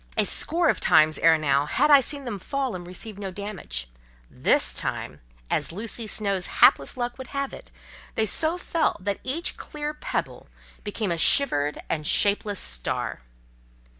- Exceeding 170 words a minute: No, average, 160 wpm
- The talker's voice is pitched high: Yes, high, 205 Hz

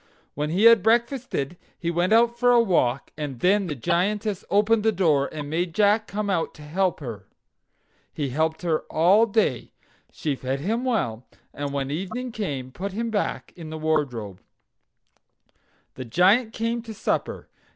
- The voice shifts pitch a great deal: Yes, wide, 6.9 semitones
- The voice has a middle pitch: Yes, medium, 180 Hz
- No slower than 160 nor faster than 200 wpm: Yes, average, 170 wpm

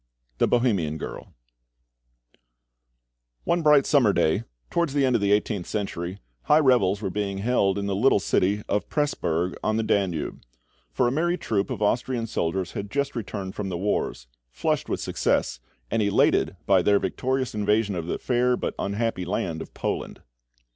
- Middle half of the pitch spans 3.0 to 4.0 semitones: No, average, 4.5 semitones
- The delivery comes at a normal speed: Yes, average, 170 wpm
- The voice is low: Yes, low, 105 Hz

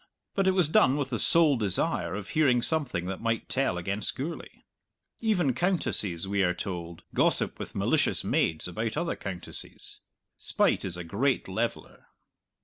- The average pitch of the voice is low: Yes, low, 115 Hz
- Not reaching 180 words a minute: Yes, average, 155 wpm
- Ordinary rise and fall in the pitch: No, wide, 8.3 semitones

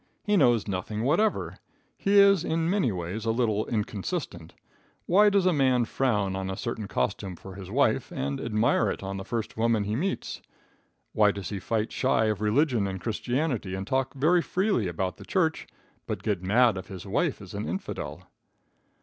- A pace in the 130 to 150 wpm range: No, average, 185 wpm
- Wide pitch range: Yes, wide, 6.7 semitones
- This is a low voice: Yes, low, 110 Hz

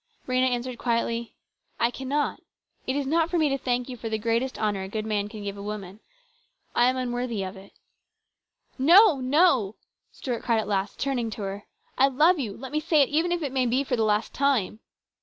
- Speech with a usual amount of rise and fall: Yes, average, 4.3 semitones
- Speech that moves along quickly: Yes, fast, 230 wpm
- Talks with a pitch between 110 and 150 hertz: No, high, 245 Hz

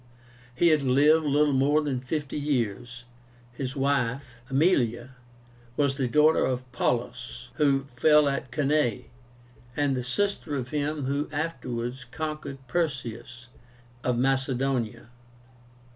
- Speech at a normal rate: No, slow, 115 wpm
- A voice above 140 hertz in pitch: No, low, 135 Hz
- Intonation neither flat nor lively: Yes, average, 3.0 semitones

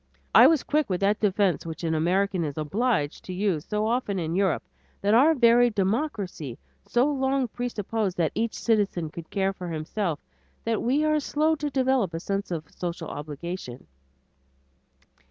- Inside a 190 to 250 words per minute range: No, average, 165 wpm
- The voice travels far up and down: Yes, wide, 6.1 semitones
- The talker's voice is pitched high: Yes, high, 200 Hz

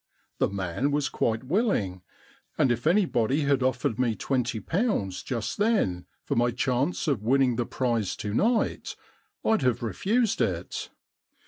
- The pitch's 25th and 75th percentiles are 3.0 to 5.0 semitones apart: No, wide, 5.5 semitones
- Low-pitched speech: Yes, low, 125 Hz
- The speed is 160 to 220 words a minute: No, average, 145 wpm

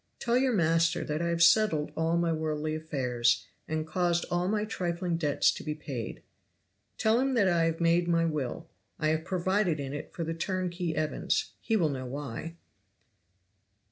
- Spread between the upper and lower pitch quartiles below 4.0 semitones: Yes, narrow, 2.6 semitones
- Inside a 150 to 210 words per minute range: Yes, average, 175 wpm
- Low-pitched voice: No, medium, 165 Hz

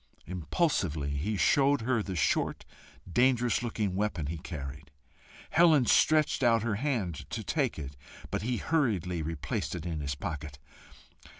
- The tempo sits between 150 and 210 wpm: No, average, 140 wpm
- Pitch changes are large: Yes, wide, 7.9 semitones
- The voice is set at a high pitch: No, very low, 95 Hz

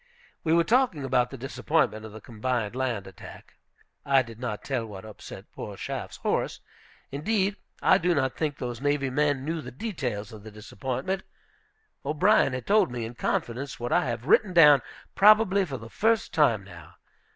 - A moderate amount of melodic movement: No, wide, 6.0 semitones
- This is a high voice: No, low, 130 Hz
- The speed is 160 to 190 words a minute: Yes, average, 175 wpm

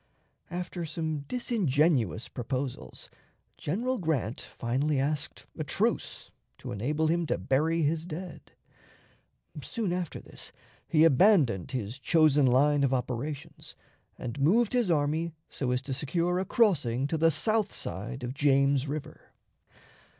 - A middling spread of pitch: Yes, average, 4.3 semitones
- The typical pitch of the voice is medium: Yes, medium, 150 Hz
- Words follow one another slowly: Yes, slow, 130 wpm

